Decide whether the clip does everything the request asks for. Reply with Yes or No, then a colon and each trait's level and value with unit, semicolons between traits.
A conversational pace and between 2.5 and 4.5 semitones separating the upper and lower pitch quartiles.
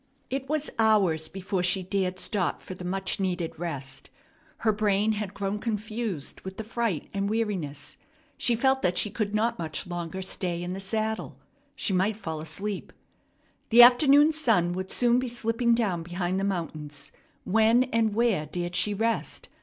Yes: average, 170 wpm; average, 4.1 semitones